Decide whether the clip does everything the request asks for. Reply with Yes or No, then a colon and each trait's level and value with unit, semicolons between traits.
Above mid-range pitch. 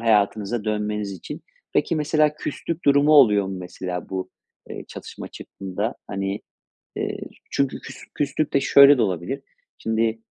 No: low, 110 Hz